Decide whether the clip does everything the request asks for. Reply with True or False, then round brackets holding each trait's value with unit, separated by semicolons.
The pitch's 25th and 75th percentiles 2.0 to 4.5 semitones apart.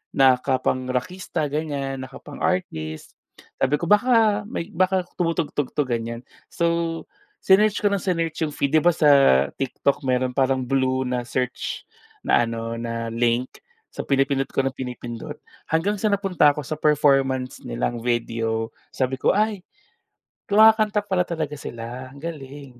False (5.2 semitones)